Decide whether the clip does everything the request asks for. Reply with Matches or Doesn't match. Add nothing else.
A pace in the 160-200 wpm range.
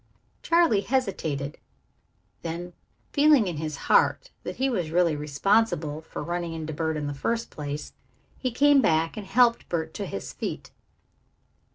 Doesn't match